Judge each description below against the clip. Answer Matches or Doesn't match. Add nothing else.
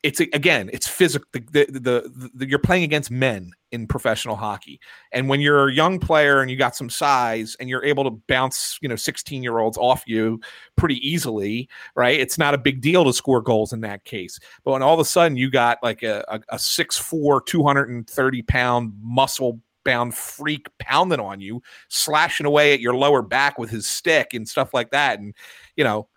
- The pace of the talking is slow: Doesn't match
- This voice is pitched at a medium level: Doesn't match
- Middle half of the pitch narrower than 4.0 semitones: Matches